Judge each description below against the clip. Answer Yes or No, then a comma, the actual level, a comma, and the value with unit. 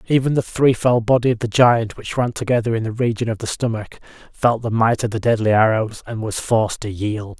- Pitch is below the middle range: Yes, low, 115 Hz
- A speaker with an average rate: No, fast, 225 wpm